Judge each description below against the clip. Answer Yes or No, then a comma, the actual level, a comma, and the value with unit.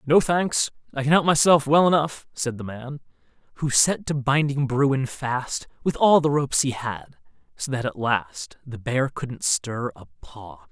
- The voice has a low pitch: Yes, low, 130 Hz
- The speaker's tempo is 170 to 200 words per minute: Yes, average, 185 wpm